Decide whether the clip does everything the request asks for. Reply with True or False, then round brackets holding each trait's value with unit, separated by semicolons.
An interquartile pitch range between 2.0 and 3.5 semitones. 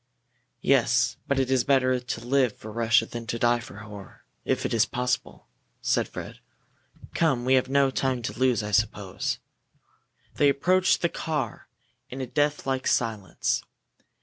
True (2.8 semitones)